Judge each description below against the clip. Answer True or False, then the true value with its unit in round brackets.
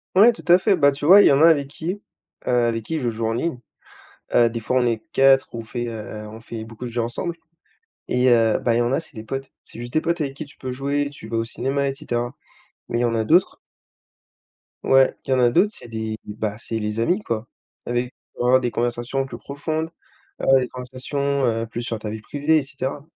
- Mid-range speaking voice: False (125 Hz)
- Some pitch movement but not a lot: True (3.6 semitones)